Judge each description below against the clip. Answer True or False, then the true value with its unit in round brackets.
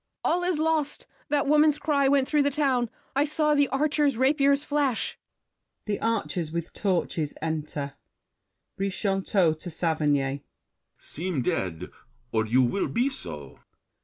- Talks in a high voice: True (230 Hz)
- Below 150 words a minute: True (135 wpm)